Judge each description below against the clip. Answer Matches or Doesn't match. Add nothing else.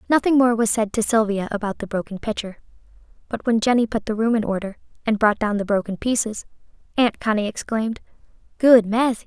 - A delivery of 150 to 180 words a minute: Doesn't match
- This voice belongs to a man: Doesn't match